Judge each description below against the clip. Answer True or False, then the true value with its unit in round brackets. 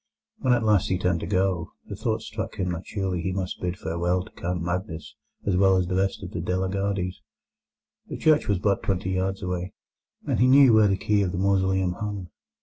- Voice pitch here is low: True (95 Hz)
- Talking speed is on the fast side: True (225 wpm)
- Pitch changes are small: True (1.7 semitones)